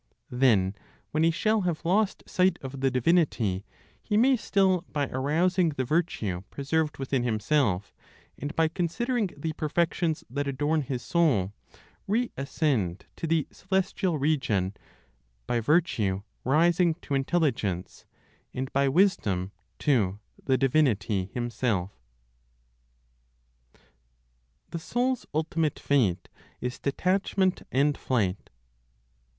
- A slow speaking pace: Yes, slow, 110 wpm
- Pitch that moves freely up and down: Yes, wide, 6.1 semitones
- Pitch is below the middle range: No, medium, 145 Hz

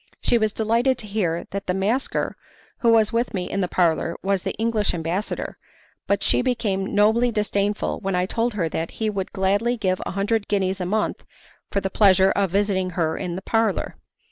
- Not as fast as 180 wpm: No, average, 195 wpm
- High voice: Yes, high, 200 Hz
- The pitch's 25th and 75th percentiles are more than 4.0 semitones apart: No, average, 2.8 semitones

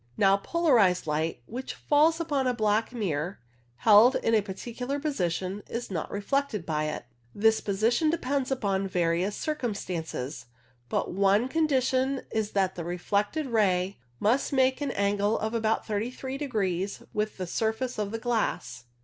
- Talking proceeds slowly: No, average, 150 wpm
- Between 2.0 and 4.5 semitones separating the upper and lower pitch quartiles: No, average, 5.2 semitones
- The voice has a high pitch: Yes, high, 215 Hz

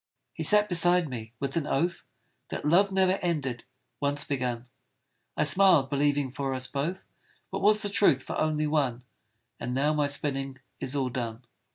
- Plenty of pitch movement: No, average, 4.6 semitones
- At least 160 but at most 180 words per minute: Yes, average, 170 wpm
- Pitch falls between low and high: Yes, medium, 145 Hz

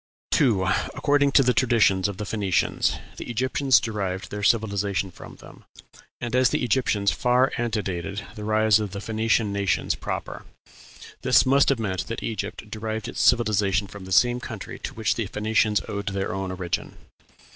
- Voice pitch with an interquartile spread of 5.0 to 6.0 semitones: No, average, 3.1 semitones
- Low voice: Yes, low, 105 Hz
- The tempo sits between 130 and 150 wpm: No, average, 165 wpm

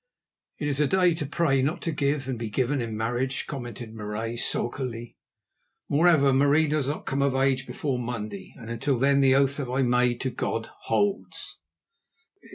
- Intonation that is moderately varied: Yes, average, 3.1 semitones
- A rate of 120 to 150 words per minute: No, average, 175 wpm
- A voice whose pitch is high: No, low, 135 Hz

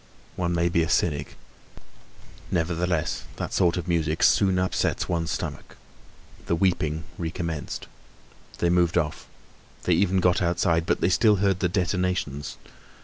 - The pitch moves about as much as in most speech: No, narrow, 1.8 semitones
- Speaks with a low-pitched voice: Yes, very low, 85 Hz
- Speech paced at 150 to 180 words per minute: No, average, 140 wpm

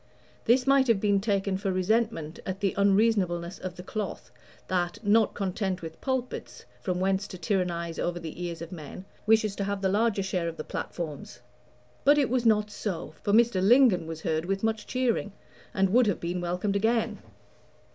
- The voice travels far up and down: No, average, 3.9 semitones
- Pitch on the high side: Yes, high, 195 Hz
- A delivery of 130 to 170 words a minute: No, average, 185 wpm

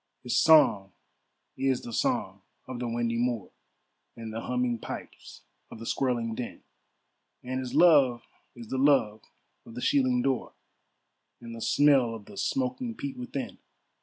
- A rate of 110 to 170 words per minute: Yes, average, 150 wpm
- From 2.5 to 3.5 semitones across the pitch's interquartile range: Yes, average, 3.0 semitones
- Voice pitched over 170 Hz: No, low, 125 Hz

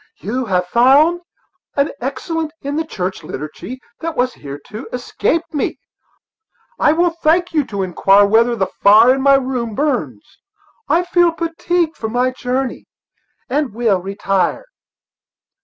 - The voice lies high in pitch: Yes, very high, 255 Hz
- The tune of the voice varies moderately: No, wide, 7.1 semitones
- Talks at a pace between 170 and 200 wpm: No, average, 140 wpm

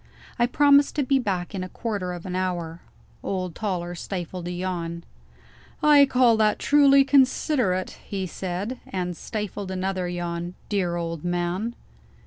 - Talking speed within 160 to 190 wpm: No, average, 145 wpm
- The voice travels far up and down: No, average, 4.9 semitones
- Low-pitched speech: No, medium, 185 Hz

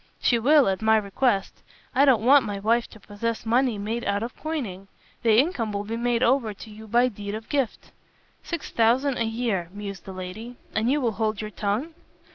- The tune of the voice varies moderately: Yes, average, 3.2 semitones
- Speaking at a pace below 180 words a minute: No, fast, 205 wpm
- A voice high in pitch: Yes, high, 225 Hz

